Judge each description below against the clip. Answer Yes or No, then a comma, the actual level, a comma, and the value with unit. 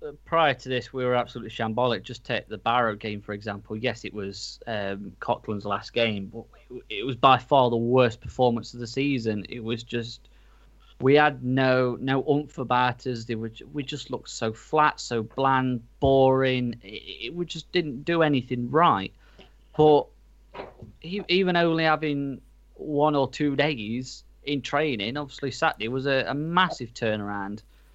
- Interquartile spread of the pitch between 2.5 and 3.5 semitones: No, average, 4.1 semitones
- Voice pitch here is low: Yes, low, 125 Hz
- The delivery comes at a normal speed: Yes, average, 165 wpm